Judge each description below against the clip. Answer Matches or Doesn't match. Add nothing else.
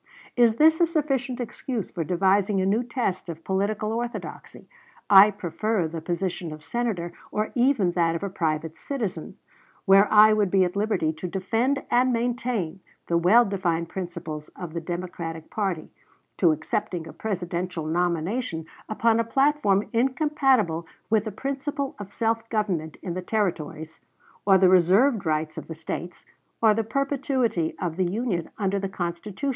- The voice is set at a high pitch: Matches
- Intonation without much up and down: Doesn't match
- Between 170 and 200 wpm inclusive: Doesn't match